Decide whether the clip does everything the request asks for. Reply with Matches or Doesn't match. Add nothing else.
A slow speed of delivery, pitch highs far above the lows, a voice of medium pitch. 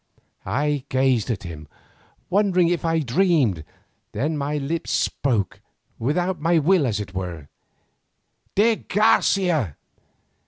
Matches